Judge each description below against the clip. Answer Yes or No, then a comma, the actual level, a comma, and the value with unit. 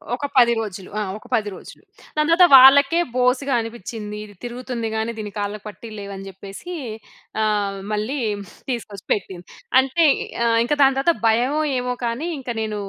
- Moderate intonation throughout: Yes, average, 4.2 semitones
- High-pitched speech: Yes, high, 230 Hz